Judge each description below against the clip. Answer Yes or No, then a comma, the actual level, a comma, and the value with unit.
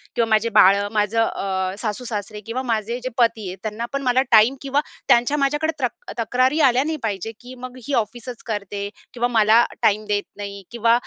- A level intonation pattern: No, average, 3.2 semitones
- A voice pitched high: Yes, high, 230 Hz